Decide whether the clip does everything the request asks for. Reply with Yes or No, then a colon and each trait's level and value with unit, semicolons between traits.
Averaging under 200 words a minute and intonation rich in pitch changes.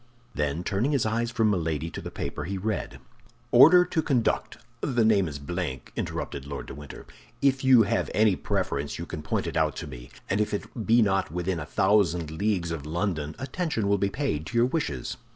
No: fast, 205 wpm; wide, 6.6 semitones